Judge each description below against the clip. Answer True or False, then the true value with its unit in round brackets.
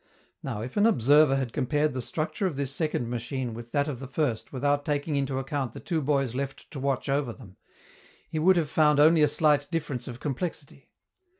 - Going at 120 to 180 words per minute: False (205 wpm)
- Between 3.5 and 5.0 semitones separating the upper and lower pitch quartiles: False (2.8 semitones)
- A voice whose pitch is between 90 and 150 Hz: True (140 Hz)